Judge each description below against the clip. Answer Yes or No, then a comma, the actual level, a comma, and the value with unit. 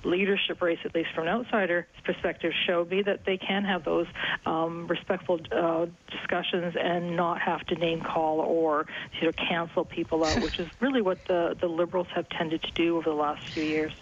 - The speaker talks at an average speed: Yes, average, 195 wpm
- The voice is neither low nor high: Yes, medium, 170 Hz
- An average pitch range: No, narrow, 1.8 semitones